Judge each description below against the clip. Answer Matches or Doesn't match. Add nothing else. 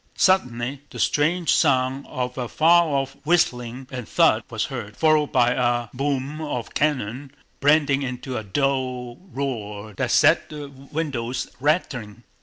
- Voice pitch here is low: Matches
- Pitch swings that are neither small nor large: Matches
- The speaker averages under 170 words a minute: Matches